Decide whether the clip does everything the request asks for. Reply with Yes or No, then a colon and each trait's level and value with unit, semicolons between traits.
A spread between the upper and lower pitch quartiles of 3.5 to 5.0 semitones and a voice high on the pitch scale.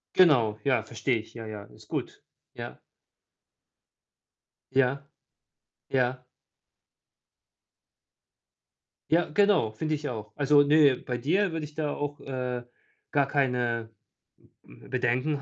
No: average, 3.8 semitones; low, 135 Hz